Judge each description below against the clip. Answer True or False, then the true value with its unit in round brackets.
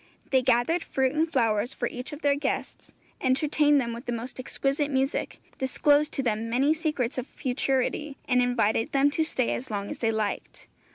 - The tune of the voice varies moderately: True (3.2 semitones)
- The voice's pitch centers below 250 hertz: False (260 Hz)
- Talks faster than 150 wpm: True (185 wpm)